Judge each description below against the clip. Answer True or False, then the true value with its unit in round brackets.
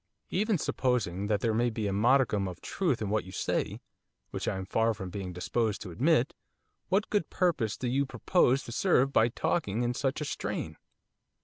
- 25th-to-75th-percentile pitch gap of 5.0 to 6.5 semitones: True (5.3 semitones)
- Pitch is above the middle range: False (120 Hz)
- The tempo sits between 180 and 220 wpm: True (195 wpm)